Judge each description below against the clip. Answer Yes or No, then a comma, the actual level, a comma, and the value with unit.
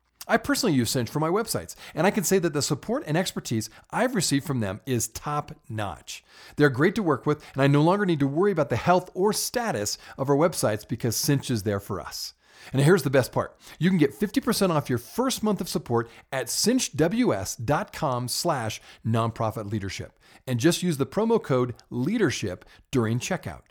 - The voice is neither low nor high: Yes, medium, 145 Hz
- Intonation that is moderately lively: No, wide, 7.3 semitones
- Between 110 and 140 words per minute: No, average, 195 wpm